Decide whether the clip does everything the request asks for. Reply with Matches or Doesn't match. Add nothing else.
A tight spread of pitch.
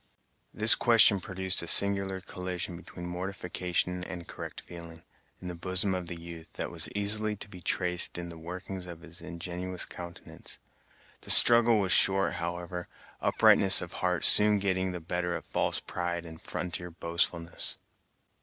Matches